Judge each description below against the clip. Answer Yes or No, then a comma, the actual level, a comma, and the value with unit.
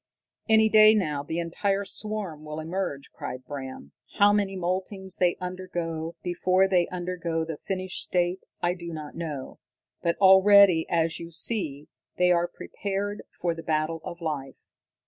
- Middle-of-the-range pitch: Yes, medium, 175 Hz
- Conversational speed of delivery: Yes, average, 150 wpm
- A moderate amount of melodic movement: Yes, average, 3.0 semitones